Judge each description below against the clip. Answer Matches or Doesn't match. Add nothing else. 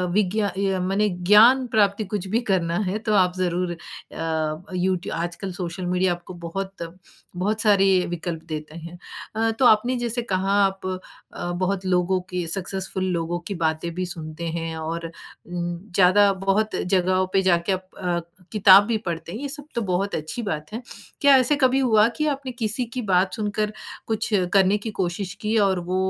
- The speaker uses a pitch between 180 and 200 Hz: Matches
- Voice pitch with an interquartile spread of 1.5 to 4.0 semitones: Matches